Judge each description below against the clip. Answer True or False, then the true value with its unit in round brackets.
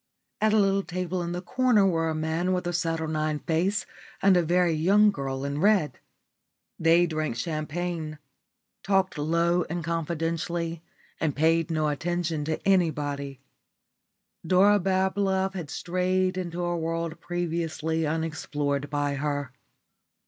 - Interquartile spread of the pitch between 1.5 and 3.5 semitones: True (2.7 semitones)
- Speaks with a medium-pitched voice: True (165 Hz)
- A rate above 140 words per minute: False (135 wpm)